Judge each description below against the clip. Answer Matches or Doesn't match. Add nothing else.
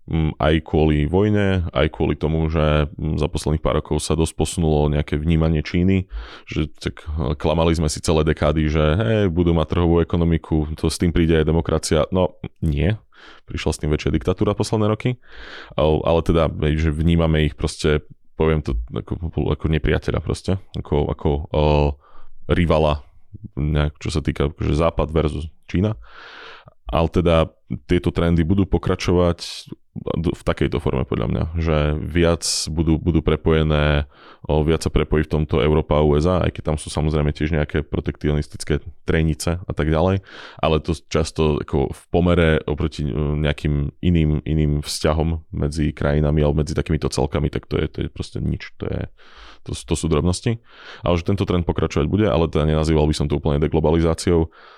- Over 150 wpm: Matches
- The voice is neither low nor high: Doesn't match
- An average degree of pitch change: Doesn't match